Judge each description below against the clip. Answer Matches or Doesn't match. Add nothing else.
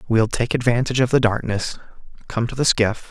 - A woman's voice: Doesn't match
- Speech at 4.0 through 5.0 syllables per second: Doesn't match